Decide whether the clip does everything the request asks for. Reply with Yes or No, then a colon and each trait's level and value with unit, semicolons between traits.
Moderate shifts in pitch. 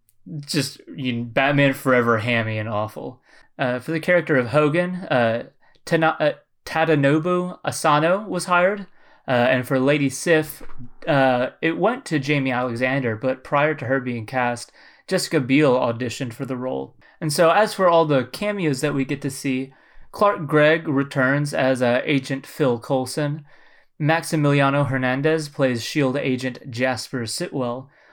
Yes: average, 3.6 semitones